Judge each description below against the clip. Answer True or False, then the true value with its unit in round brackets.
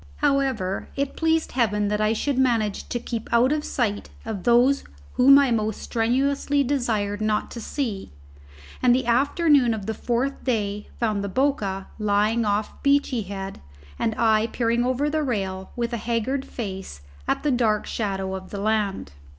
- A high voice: True (230 Hz)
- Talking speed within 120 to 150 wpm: False (165 wpm)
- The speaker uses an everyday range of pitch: True (4.1 semitones)